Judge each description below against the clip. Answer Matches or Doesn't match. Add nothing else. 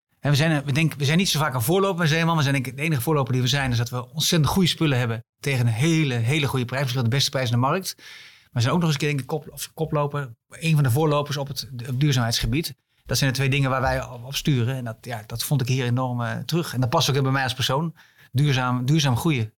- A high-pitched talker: Doesn't match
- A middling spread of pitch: Matches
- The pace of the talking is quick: Matches